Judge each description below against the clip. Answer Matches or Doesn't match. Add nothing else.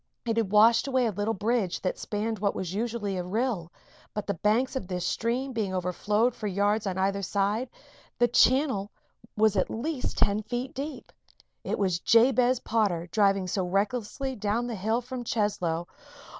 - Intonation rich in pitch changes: Doesn't match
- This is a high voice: Matches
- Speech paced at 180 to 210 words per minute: Doesn't match